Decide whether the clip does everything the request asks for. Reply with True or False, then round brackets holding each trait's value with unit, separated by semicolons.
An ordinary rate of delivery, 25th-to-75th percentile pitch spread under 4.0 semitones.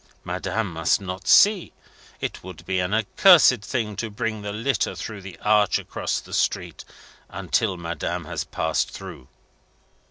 True (150 wpm; 3.6 semitones)